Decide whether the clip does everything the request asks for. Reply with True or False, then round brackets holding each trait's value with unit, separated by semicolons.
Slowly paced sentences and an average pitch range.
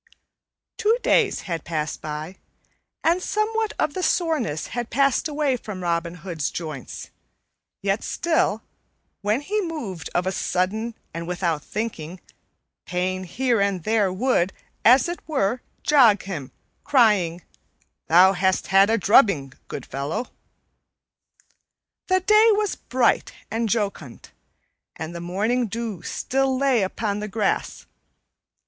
False (130 wpm; 6.9 semitones)